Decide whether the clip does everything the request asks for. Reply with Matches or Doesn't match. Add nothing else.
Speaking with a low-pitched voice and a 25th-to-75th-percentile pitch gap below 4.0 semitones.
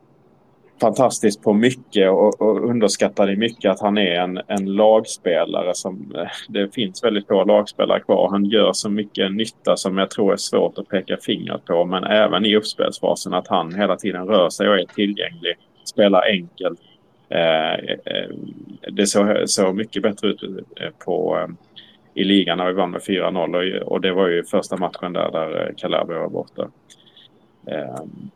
Matches